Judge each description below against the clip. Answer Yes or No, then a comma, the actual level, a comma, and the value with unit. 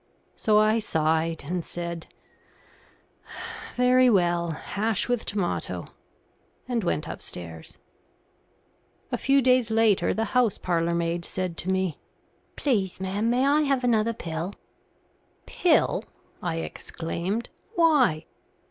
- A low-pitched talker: No, high, 200 Hz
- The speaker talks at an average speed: No, slow, 110 wpm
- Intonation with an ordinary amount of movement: No, wide, 6.1 semitones